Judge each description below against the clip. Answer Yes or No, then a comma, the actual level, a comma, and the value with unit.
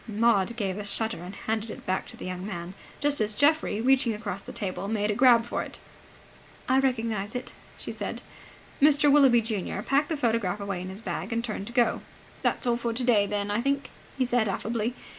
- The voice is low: No, high, 225 Hz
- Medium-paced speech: No, fast, 210 wpm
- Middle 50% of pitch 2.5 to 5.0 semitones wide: Yes, average, 3.5 semitones